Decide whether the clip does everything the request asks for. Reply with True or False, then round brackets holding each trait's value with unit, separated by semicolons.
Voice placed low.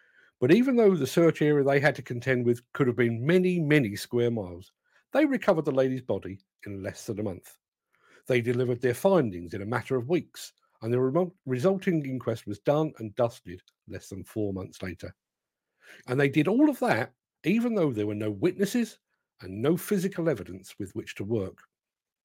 True (130 Hz)